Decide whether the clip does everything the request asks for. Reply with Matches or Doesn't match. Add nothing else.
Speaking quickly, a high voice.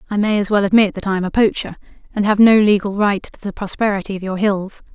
Matches